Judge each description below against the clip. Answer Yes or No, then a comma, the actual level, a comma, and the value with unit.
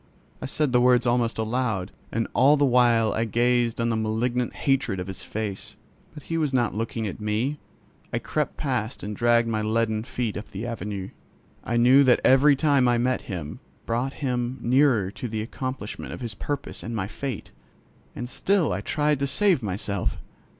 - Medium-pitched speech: No, low, 120 Hz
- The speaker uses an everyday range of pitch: Yes, average, 3.1 semitones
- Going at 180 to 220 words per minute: Yes, average, 185 wpm